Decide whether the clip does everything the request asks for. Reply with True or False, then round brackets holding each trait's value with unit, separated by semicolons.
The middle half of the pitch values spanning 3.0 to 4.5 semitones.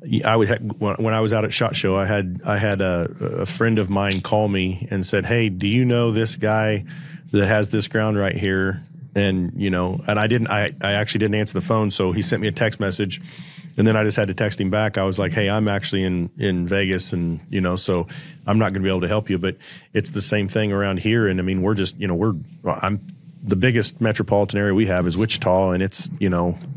False (2.5 semitones)